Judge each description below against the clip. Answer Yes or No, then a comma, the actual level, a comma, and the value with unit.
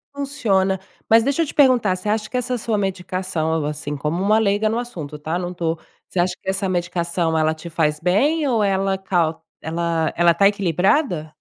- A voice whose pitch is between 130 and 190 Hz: Yes, medium, 185 Hz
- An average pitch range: Yes, average, 4.6 semitones